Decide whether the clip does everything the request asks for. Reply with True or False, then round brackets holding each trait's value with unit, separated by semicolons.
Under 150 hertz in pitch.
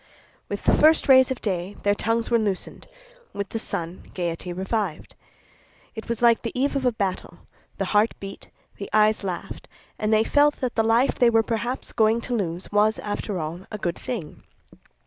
False (215 Hz)